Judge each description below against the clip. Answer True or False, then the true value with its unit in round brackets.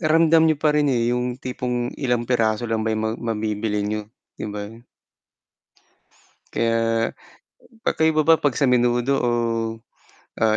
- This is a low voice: True (120 Hz)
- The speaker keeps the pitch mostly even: False (4.0 semitones)